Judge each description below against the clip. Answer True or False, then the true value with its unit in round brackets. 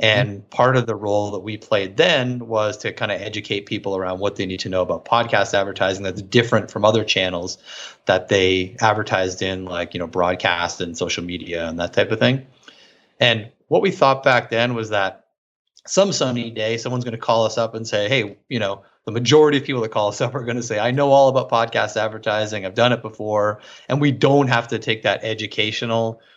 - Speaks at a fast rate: True (220 wpm)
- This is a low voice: True (110 Hz)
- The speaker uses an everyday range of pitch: True (3.6 semitones)